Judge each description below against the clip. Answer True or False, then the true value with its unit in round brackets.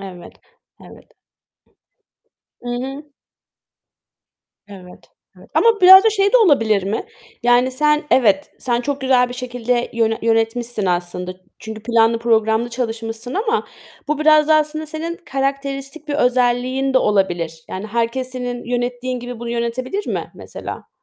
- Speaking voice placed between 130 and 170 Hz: False (245 Hz)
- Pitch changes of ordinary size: True (3.7 semitones)